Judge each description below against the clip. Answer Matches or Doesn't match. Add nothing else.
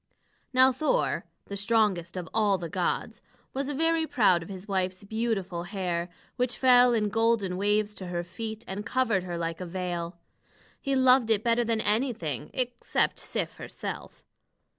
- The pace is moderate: Matches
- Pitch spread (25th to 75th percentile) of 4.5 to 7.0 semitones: Matches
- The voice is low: Doesn't match